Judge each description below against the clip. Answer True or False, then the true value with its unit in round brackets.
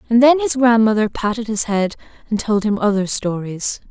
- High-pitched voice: True (220 Hz)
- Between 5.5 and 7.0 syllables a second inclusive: False (5.1 syllables/s)